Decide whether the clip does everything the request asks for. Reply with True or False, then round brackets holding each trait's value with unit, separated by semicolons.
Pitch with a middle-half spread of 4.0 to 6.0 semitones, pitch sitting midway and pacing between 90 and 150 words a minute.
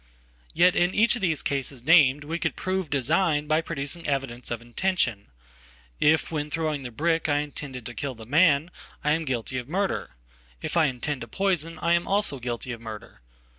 False (4.6 semitones; 150 Hz; 175 wpm)